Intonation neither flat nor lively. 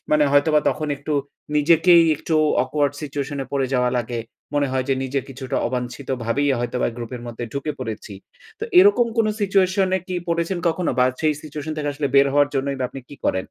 Yes: average, 3.4 semitones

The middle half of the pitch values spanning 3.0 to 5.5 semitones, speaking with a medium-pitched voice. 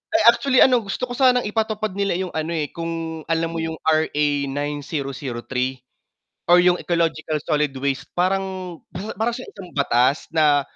Yes: average, 4.9 semitones; medium, 165 Hz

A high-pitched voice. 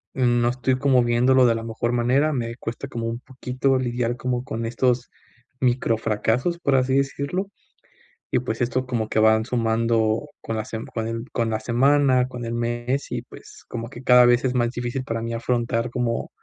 No: low, 120 Hz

